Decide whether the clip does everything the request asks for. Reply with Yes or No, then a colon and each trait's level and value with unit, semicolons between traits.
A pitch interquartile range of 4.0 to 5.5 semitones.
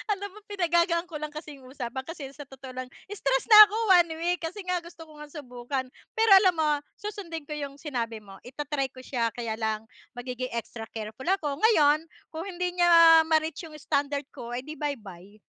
Yes: average, 4.9 semitones